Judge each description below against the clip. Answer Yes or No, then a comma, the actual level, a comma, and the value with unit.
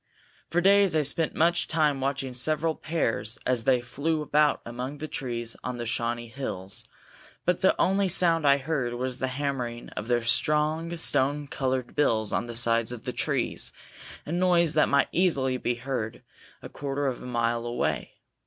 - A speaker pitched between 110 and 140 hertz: Yes, low, 135 Hz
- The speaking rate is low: No, average, 175 wpm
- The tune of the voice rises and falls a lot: No, average, 4.6 semitones